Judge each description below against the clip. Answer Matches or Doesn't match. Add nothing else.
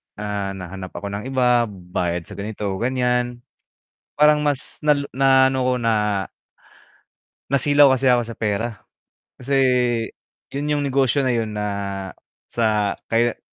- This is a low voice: Matches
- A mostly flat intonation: Doesn't match